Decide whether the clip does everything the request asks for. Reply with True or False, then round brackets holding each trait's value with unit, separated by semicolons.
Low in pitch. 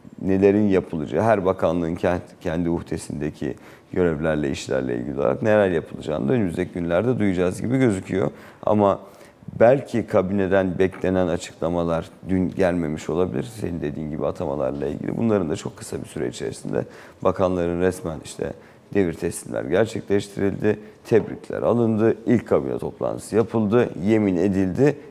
True (95 Hz)